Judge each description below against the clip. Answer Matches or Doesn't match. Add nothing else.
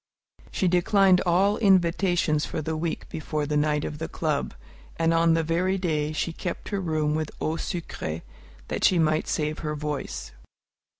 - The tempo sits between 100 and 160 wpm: Doesn't match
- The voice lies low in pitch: Doesn't match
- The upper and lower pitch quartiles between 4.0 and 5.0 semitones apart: Doesn't match